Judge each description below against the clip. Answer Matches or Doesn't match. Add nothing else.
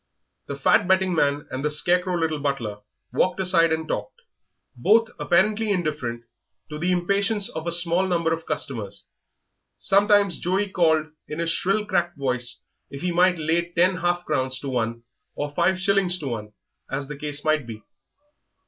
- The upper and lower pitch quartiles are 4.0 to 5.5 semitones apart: Matches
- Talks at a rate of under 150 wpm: Doesn't match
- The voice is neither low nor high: Matches